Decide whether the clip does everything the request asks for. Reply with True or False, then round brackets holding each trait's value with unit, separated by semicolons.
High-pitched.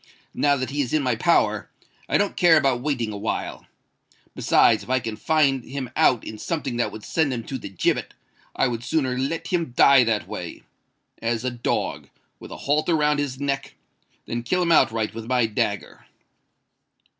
False (130 Hz)